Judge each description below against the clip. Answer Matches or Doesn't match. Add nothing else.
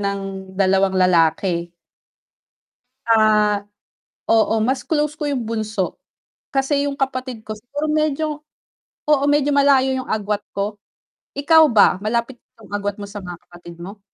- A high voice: Matches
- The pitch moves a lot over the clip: Matches